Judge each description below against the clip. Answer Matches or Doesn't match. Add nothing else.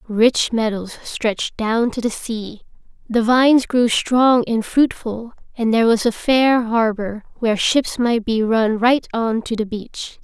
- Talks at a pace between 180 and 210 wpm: Doesn't match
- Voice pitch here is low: Doesn't match